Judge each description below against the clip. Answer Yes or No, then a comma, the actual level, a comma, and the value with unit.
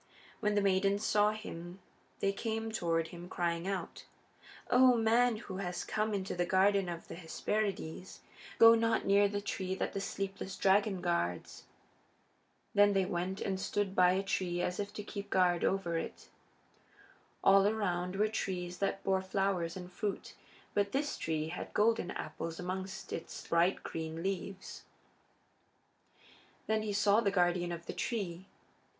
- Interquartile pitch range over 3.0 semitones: No, narrow, 2.5 semitones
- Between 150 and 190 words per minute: Yes, average, 155 wpm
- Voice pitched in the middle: No, high, 195 Hz